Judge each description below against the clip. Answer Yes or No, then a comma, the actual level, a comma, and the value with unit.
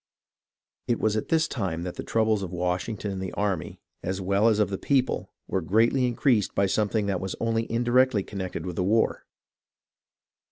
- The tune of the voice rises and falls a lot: No, average, 3.4 semitones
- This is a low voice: Yes, low, 105 Hz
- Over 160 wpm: Yes, average, 185 wpm